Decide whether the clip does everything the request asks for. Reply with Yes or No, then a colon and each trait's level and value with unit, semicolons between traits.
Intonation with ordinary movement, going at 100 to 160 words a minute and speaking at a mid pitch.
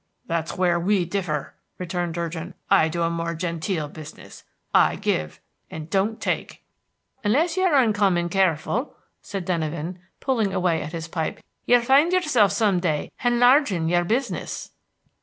Yes: average, 4.8 semitones; average, 140 wpm; medium, 180 Hz